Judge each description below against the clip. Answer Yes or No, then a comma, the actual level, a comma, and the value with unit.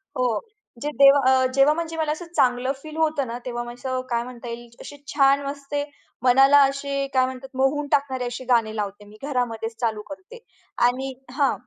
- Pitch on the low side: No, very high, 265 Hz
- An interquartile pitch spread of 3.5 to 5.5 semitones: No, average, 2.7 semitones